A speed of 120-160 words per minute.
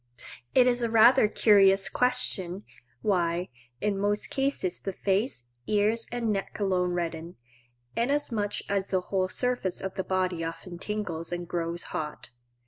Yes: average, 140 wpm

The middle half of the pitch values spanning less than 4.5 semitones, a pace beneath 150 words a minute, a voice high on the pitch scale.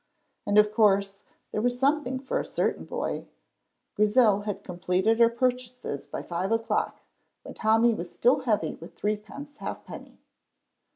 Yes: average, 3.8 semitones; average, 140 wpm; high, 220 Hz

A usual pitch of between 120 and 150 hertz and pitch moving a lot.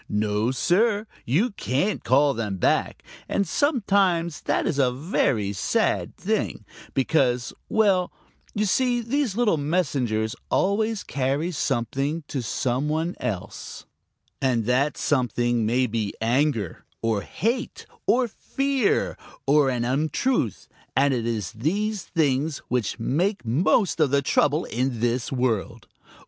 Yes: medium, 140 Hz; wide, 7.6 semitones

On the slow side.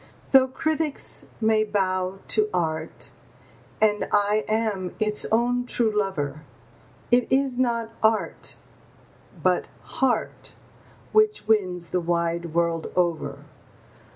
Yes: slow, 105 wpm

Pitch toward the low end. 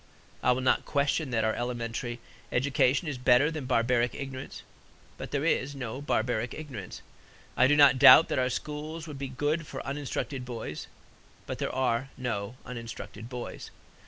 Yes: low, 130 Hz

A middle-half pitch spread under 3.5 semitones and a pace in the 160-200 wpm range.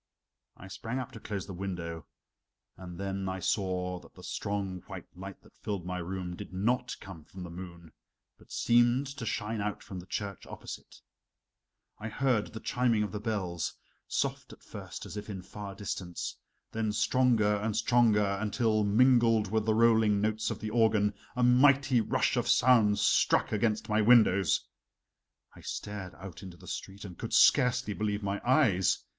Yes: average, 3.0 semitones; average, 175 wpm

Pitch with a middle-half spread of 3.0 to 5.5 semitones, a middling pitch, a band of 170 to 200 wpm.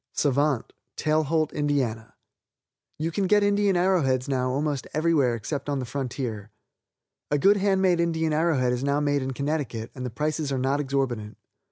Yes: average, 3.8 semitones; medium, 145 Hz; average, 175 wpm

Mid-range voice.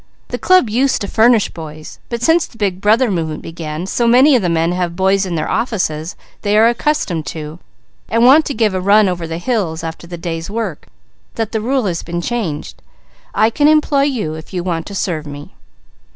No: high, 195 Hz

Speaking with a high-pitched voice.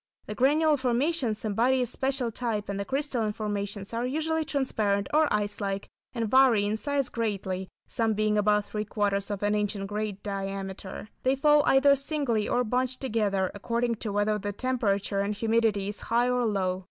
Yes: high, 215 Hz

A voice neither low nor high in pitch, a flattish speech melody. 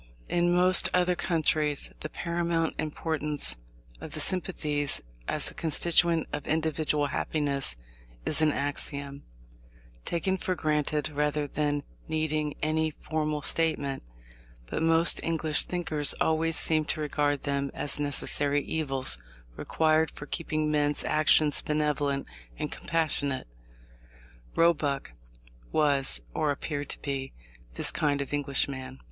Yes: medium, 150 Hz; narrow, 1.9 semitones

